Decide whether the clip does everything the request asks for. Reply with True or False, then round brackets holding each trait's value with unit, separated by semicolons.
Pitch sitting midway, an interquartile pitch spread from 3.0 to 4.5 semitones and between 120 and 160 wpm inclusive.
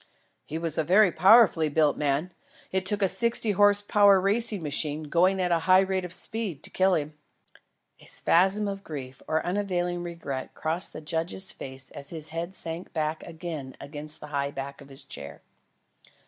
False (170 Hz; 4.1 semitones; 180 wpm)